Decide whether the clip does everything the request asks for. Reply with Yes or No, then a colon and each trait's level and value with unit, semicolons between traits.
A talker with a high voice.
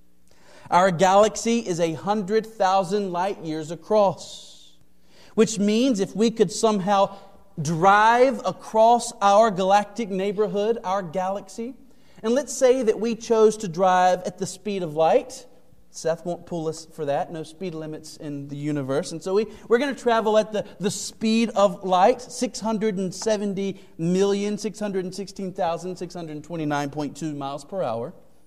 Yes: high, 195 Hz